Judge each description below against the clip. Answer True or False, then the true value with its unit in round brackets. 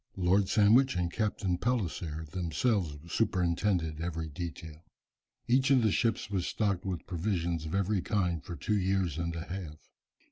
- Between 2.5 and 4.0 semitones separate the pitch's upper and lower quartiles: True (3.6 semitones)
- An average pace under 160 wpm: True (150 wpm)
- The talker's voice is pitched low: True (90 Hz)